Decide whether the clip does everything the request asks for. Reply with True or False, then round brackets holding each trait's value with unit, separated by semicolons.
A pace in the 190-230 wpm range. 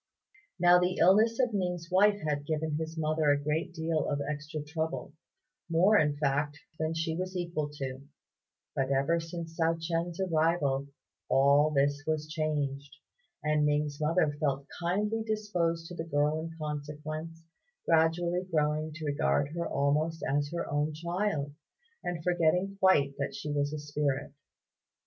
False (150 wpm)